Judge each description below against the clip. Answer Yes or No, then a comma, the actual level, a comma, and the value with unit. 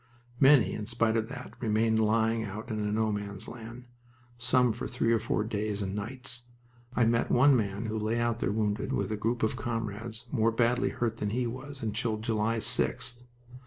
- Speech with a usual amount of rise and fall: No, narrow, 1.9 semitones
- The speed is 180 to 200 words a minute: Yes, average, 190 wpm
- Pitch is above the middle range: No, low, 115 Hz